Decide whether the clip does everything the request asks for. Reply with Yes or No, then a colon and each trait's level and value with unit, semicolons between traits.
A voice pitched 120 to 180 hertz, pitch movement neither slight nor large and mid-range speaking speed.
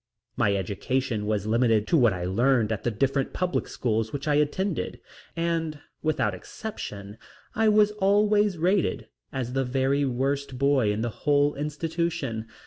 No: low, 135 Hz; wide, 6.6 semitones; average, 150 wpm